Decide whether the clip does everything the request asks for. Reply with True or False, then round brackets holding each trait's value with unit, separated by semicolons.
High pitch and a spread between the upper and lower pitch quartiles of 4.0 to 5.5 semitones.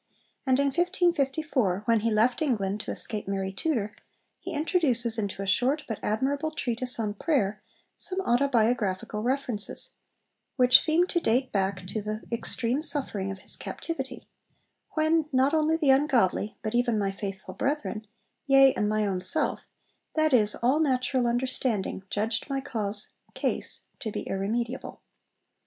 True (240 Hz; 5.0 semitones)